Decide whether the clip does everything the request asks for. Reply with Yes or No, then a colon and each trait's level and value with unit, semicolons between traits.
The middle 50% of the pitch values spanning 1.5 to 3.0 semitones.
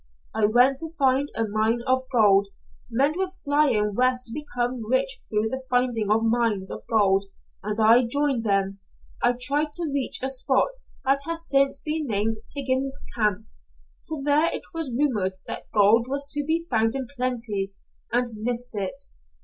No: average, 4.2 semitones